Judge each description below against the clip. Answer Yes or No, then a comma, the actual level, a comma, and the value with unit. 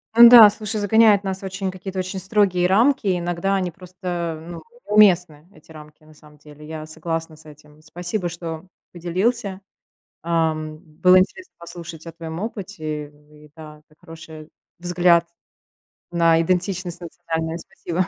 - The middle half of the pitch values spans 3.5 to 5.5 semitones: No, average, 2.9 semitones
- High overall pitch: No, medium, 175 Hz